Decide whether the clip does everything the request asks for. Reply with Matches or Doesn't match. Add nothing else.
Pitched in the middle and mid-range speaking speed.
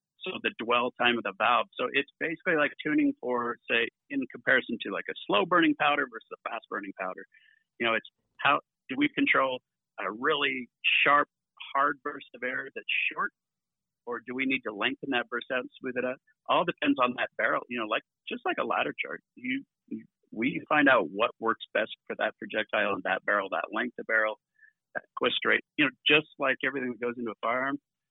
Doesn't match